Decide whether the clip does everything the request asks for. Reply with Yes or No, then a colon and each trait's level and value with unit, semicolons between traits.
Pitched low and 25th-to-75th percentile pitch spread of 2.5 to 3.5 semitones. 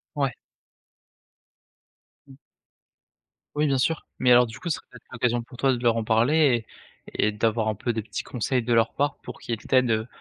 Yes: low, 120 Hz; average, 2.9 semitones